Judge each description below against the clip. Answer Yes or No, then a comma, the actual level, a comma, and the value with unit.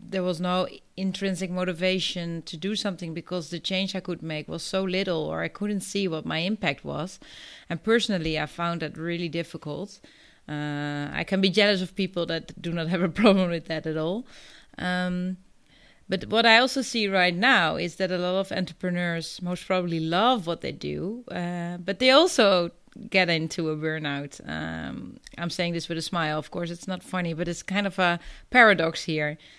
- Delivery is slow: No, average, 195 wpm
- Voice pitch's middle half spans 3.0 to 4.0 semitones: No, narrow, 2.5 semitones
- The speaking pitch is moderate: Yes, medium, 180 Hz